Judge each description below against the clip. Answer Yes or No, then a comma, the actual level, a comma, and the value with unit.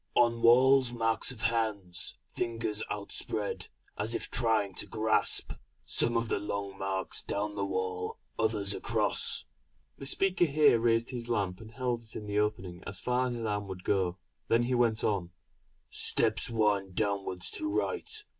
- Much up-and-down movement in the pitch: No, average, 2.9 semitones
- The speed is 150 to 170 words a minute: Yes, average, 165 wpm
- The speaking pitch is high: No, low, 110 Hz